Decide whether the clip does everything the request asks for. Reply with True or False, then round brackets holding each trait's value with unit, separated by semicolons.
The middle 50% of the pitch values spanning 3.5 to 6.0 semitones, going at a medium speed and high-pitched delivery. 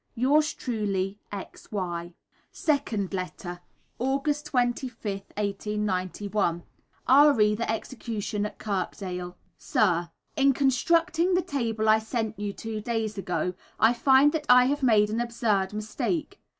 False (4.7 semitones; 125 wpm; 220 Hz)